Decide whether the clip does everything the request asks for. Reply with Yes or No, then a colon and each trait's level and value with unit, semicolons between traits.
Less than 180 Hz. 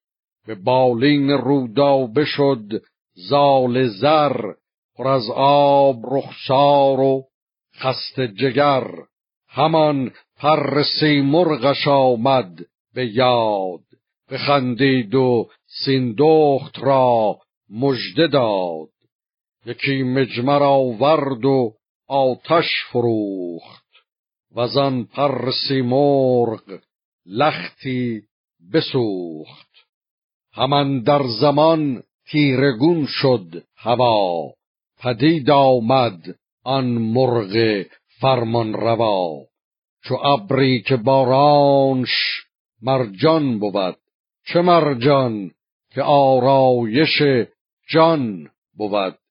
Yes: low, 135 Hz